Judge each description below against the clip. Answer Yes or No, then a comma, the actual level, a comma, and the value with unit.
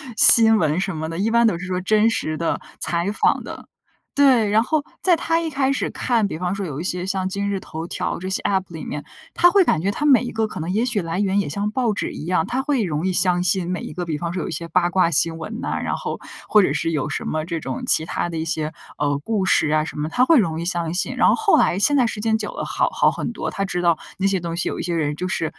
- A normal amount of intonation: Yes, average, 4.9 semitones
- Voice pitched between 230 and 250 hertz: No, medium, 185 Hz